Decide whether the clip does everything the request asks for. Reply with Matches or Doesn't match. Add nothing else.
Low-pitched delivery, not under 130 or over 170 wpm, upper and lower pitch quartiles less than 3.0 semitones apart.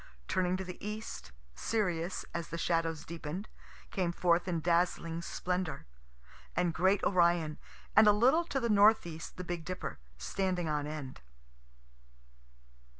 Doesn't match